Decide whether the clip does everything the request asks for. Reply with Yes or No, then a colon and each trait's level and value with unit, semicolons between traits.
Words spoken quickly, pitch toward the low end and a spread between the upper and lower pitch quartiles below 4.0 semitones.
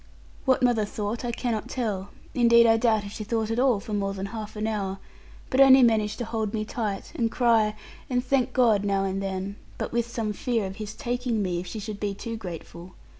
No: fast, 225 wpm; high, 220 Hz; average, 2.8 semitones